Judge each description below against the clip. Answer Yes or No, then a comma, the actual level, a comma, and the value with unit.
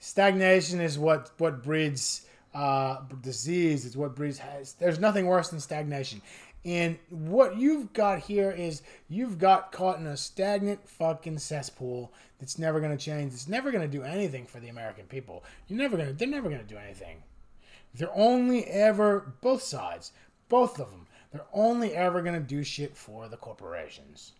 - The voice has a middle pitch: Yes, medium, 160 Hz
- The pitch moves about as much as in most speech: No, wide, 6.6 semitones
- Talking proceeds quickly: No, average, 165 wpm